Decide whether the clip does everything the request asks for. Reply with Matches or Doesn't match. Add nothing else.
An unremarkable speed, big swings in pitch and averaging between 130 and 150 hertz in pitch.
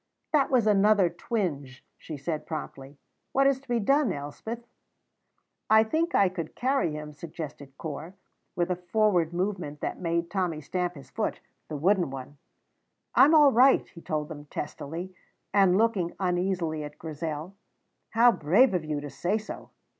Doesn't match